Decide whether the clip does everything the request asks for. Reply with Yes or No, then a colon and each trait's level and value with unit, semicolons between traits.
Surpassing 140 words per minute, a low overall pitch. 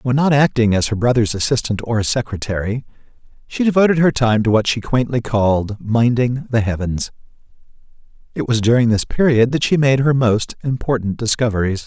Yes: average, 165 wpm; low, 120 Hz